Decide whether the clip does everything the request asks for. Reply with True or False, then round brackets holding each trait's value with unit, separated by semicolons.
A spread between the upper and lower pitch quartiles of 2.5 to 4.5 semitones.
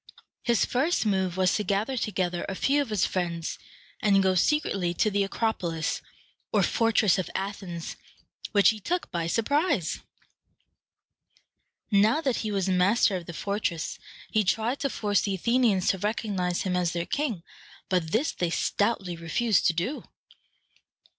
True (4.1 semitones)